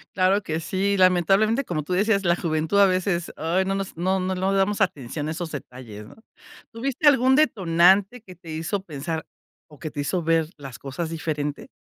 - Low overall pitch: No, medium, 180 Hz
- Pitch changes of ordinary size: Yes, average, 3.7 semitones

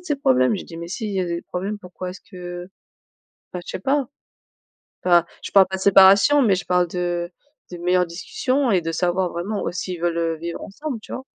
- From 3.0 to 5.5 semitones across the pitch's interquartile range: No, narrow, 2.5 semitones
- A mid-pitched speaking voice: Yes, medium, 180 Hz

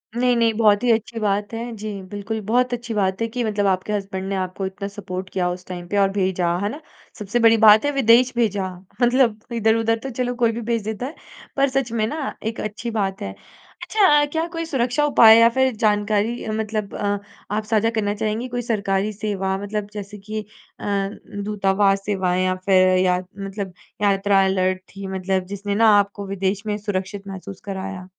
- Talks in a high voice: Yes, high, 210 Hz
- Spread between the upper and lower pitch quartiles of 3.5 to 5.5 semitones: No, average, 2.8 semitones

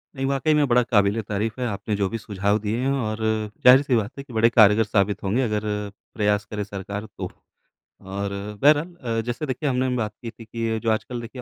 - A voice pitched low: Yes, low, 115 Hz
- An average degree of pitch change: Yes, average, 3.4 semitones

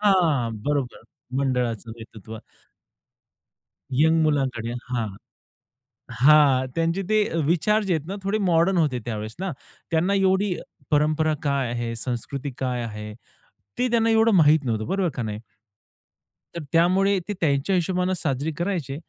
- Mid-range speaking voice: Yes, medium, 150 Hz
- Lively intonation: Yes, wide, 6.5 semitones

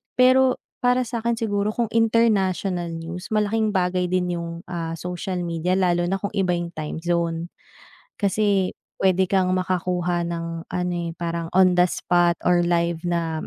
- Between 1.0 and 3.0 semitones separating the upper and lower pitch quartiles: Yes, narrow, 2.5 semitones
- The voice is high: No, medium, 180 Hz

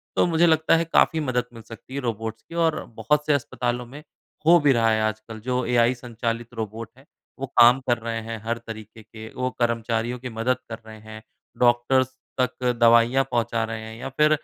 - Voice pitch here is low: Yes, low, 120 Hz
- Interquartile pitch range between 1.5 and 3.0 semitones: Yes, narrow, 2.5 semitones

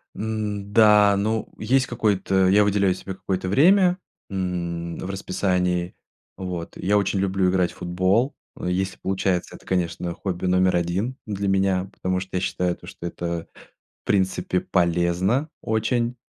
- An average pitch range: No, narrow, 2.3 semitones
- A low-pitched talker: Yes, very low, 95 Hz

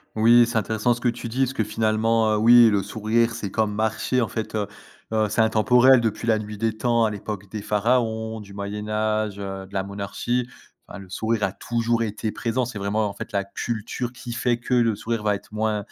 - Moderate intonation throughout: No, narrow, 1.9 semitones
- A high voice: No, low, 110 Hz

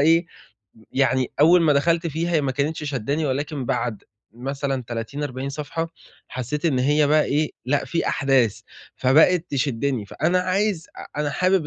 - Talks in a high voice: No, medium, 145 Hz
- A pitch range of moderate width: Yes, average, 3.6 semitones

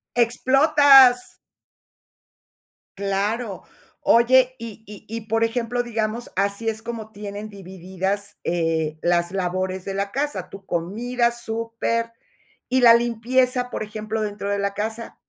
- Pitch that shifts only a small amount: No, average, 3.1 semitones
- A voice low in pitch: No, high, 220 Hz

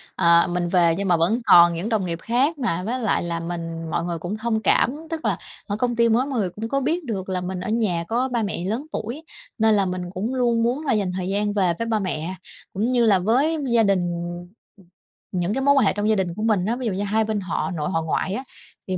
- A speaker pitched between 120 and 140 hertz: No, high, 205 Hz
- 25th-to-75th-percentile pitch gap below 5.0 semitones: Yes, average, 4.6 semitones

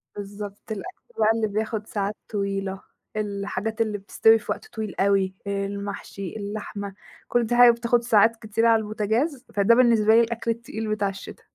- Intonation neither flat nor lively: No, narrow, 2.2 semitones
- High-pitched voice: Yes, high, 215 Hz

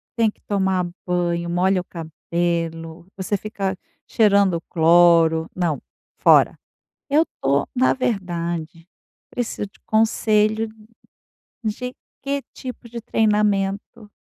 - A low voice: No, high, 190 Hz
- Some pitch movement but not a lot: Yes, average, 4.2 semitones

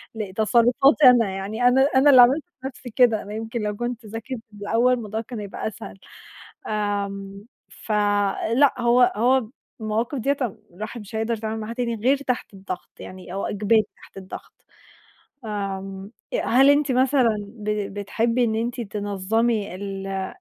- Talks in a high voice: Yes, high, 220 Hz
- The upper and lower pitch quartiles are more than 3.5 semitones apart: No, average, 3.2 semitones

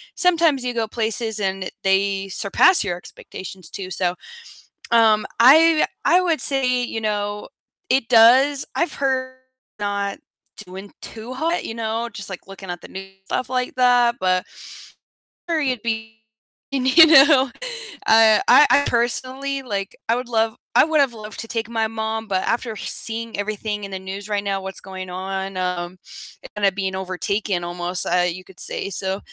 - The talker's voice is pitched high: Yes, high, 220 Hz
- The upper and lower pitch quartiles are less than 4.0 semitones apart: No, average, 4.5 semitones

